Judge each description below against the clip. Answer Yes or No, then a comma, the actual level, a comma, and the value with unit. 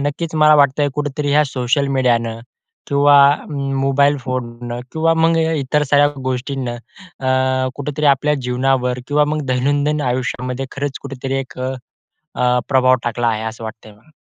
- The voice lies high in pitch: No, low, 135 Hz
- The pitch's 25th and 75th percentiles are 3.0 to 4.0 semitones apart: No, narrow, 2.4 semitones